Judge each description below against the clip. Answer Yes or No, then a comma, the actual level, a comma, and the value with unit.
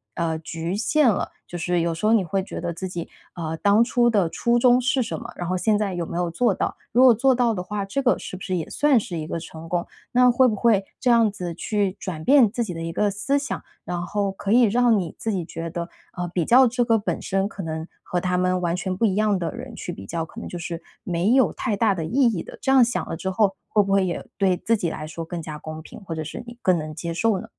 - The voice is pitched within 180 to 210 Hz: Yes, high, 190 Hz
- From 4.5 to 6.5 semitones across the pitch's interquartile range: Yes, average, 5.1 semitones